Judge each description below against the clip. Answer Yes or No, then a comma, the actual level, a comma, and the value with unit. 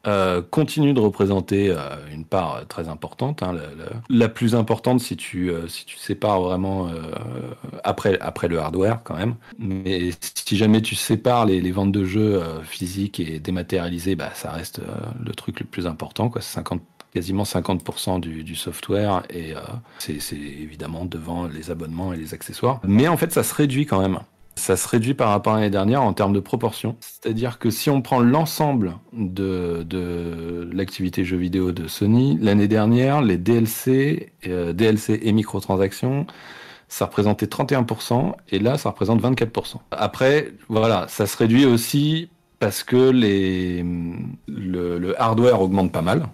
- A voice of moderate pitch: No, low, 100 Hz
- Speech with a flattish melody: No, average, 4.5 semitones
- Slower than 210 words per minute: Yes, average, 175 wpm